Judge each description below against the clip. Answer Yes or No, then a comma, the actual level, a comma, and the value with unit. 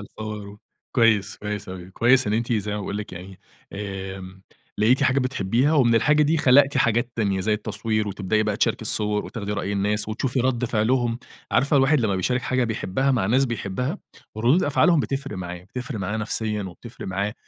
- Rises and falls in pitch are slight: No, average, 3.9 semitones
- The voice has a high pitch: No, low, 110 Hz